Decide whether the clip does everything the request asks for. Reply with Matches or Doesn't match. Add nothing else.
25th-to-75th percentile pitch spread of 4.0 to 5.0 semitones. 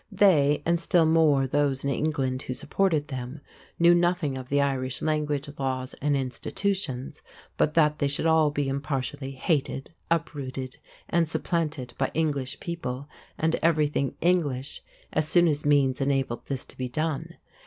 Doesn't match